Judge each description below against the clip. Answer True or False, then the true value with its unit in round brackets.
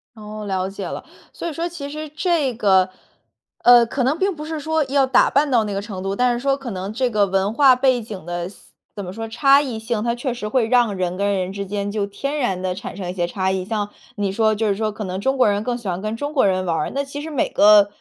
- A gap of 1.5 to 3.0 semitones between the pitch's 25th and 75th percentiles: False (5.3 semitones)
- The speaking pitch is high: True (220 Hz)